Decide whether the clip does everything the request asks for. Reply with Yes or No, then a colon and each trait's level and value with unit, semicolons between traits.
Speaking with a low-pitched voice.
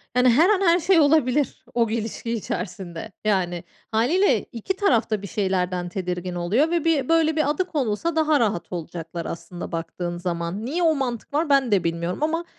No: high, 230 Hz